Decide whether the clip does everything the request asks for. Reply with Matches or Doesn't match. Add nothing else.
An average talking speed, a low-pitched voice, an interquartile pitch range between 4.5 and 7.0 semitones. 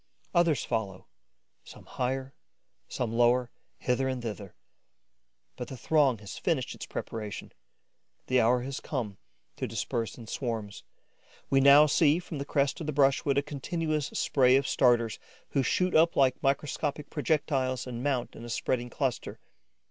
Doesn't match